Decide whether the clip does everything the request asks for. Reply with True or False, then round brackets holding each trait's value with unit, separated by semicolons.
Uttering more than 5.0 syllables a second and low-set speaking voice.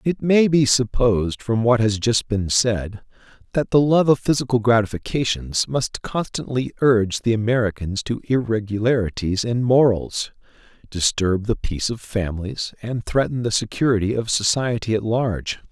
False (4.9 syllables/s; 115 Hz)